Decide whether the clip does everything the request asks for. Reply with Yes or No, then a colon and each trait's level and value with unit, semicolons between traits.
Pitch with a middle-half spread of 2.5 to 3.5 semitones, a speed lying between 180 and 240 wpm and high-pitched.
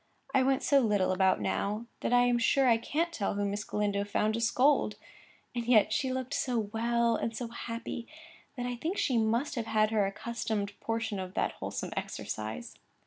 Yes: average, 2.9 semitones; average, 195 wpm; high, 230 Hz